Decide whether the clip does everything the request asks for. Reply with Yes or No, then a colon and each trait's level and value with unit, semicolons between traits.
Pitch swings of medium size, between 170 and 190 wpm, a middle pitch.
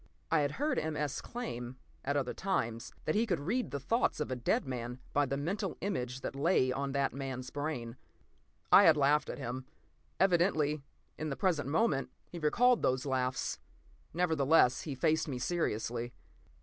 Yes: average, 4.4 semitones; average, 175 wpm; medium, 145 Hz